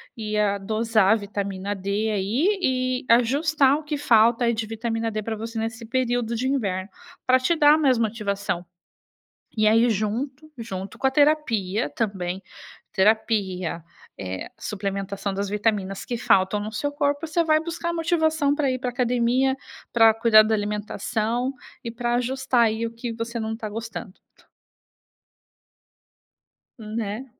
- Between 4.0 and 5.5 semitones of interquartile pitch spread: No, average, 3.6 semitones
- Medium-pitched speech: No, high, 225 Hz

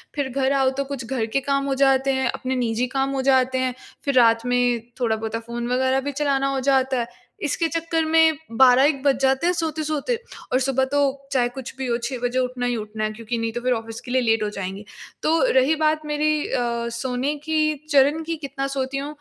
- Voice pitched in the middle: No, very high, 265 Hz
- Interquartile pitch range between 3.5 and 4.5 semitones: No, average, 2.7 semitones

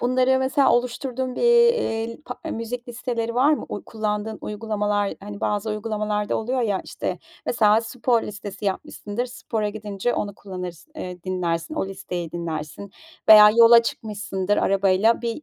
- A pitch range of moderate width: Yes, average, 3.2 semitones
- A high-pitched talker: Yes, high, 215 Hz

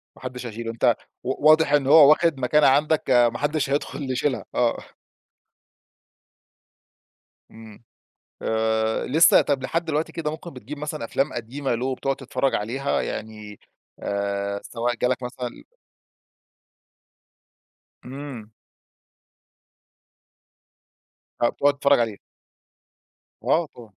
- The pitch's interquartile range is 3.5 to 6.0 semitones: Yes, average, 4.0 semitones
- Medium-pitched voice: No, low, 130 Hz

